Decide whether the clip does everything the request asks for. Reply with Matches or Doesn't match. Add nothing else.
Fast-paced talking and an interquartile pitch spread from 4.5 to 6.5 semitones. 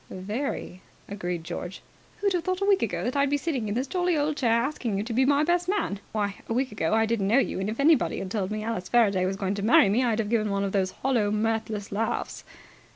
Matches